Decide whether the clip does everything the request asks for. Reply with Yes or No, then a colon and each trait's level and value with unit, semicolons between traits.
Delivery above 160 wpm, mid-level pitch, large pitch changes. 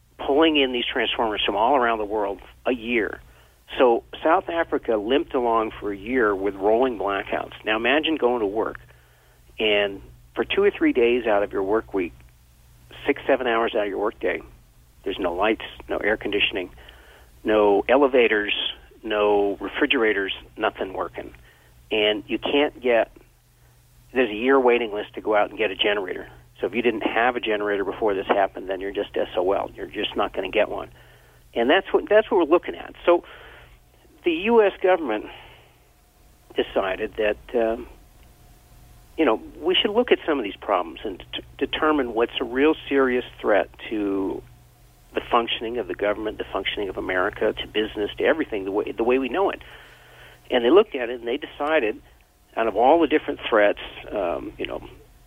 No: average, 180 wpm; low, 110 Hz; wide, 5.7 semitones